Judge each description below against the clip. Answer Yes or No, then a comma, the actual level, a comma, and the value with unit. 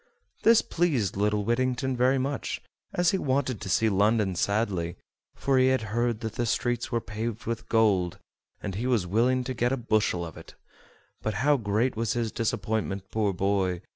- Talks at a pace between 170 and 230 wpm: Yes, average, 180 wpm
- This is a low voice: Yes, low, 115 Hz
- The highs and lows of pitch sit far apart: No, average, 3.8 semitones